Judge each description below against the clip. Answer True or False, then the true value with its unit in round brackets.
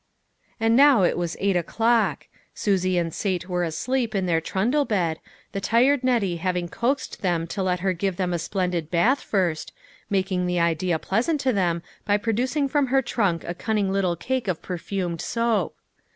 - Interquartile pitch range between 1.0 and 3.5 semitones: False (4.8 semitones)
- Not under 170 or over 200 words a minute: True (180 wpm)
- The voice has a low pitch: False (190 Hz)